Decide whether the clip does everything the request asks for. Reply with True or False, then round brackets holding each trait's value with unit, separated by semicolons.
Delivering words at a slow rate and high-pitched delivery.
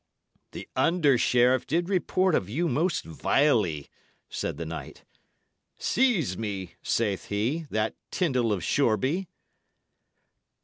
False (115 wpm; 125 Hz)